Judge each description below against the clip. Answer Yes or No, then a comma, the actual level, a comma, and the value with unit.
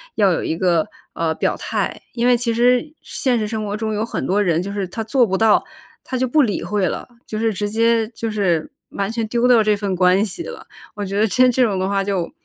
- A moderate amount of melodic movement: Yes, average, 3.2 semitones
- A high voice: Yes, high, 215 Hz